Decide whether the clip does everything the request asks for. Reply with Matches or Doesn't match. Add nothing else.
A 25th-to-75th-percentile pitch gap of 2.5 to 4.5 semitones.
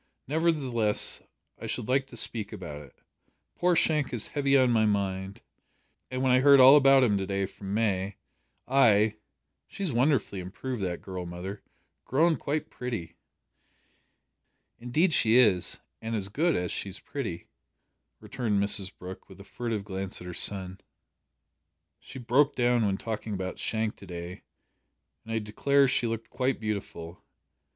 Doesn't match